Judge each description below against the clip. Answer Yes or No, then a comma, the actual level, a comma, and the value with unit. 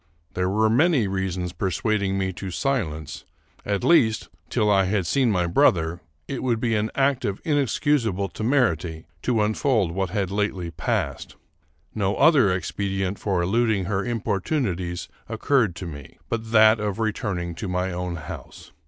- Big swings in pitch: No, average, 3.9 semitones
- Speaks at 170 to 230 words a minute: No, average, 155 wpm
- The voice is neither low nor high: No, low, 100 Hz